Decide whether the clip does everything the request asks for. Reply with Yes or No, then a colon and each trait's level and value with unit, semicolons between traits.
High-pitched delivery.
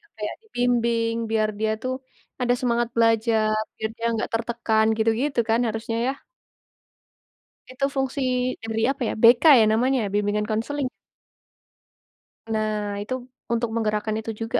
Yes: high, 225 Hz